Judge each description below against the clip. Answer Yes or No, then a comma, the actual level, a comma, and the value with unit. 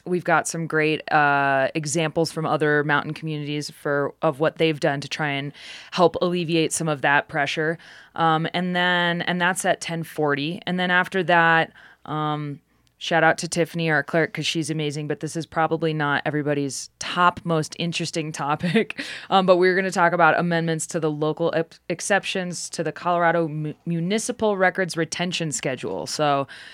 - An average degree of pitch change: No, narrow, 2.3 semitones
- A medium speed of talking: Yes, average, 170 wpm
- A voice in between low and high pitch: Yes, medium, 160 Hz